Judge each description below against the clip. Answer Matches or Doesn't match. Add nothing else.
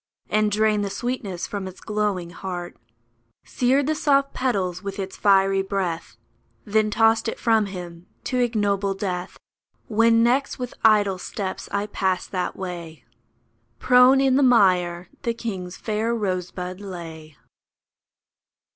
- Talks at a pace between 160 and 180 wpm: Doesn't match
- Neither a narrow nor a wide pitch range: Matches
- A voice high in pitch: Matches